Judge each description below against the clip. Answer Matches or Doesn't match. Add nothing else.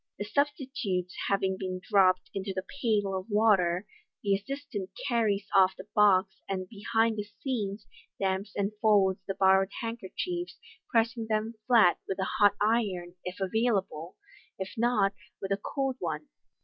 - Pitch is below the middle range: Doesn't match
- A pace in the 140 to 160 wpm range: Matches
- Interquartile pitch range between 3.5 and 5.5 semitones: Doesn't match